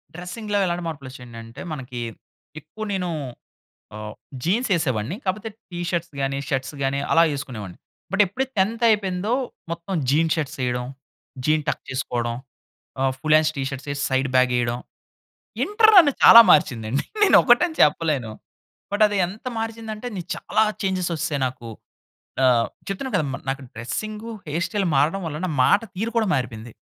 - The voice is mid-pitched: Yes, medium, 160 Hz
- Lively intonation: Yes, wide, 7.9 semitones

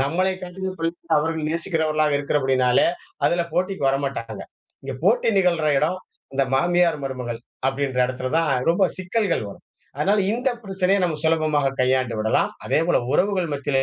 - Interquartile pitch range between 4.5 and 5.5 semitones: Yes, average, 4.9 semitones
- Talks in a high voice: No, medium, 160 Hz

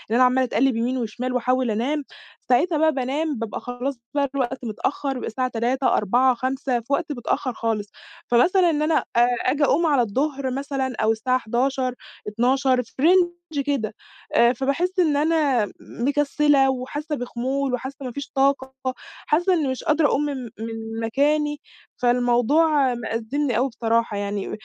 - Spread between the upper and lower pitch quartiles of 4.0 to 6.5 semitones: No, average, 3.2 semitones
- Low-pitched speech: No, very high, 260 Hz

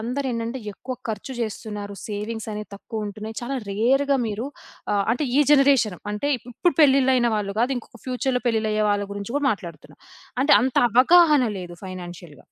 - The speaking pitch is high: Yes, high, 230 Hz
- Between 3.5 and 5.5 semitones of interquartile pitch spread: Yes, average, 4.2 semitones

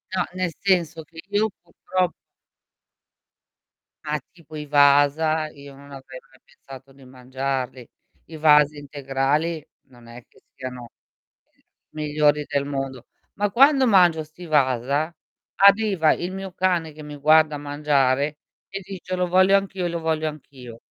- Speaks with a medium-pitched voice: Yes, medium, 150 Hz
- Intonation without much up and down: No, average, 4.1 semitones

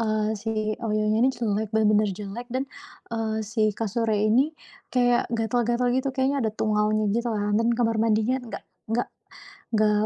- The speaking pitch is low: No, high, 225 Hz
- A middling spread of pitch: No, narrow, 2.1 semitones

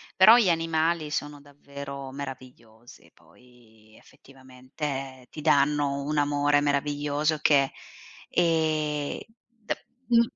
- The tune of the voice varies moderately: No, narrow, 2.3 semitones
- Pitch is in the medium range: Yes, medium, 145 Hz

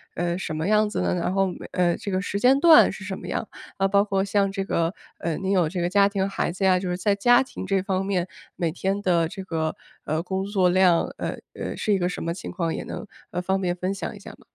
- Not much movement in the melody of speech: Yes, narrow, 2.0 semitones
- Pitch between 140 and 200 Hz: Yes, high, 190 Hz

